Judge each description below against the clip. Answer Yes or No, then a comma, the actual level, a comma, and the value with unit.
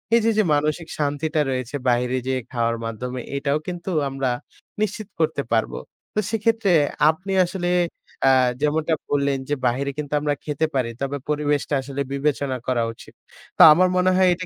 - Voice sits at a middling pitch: Yes, medium, 145 Hz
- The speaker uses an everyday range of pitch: Yes, average, 4.6 semitones